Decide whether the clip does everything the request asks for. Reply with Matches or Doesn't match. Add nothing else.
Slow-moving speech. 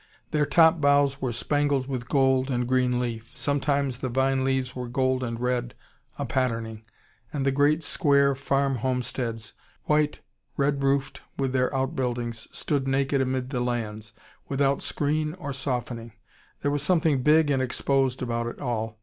Doesn't match